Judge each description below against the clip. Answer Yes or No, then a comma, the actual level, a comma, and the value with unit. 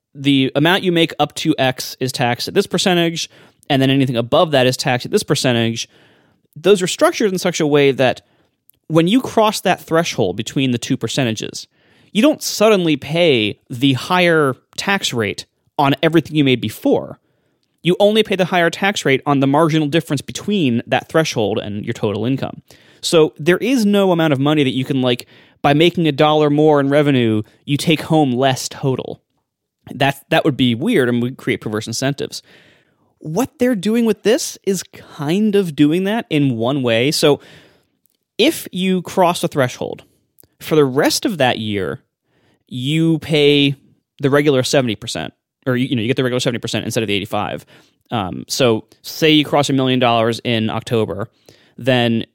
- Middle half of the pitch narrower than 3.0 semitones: No, average, 5.0 semitones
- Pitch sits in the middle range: Yes, medium, 145 Hz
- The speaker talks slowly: No, average, 180 wpm